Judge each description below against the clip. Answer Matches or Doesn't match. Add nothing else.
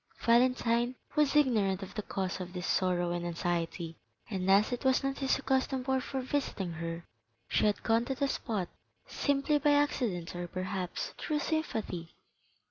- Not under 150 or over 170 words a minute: Matches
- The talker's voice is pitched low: Doesn't match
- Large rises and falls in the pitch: Matches